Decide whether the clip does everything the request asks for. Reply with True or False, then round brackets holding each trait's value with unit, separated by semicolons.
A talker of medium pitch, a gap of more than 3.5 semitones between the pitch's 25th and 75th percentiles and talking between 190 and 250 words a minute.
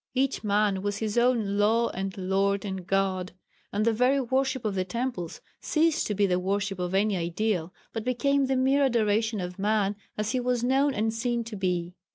False (215 Hz; 4.1 semitones; 200 wpm)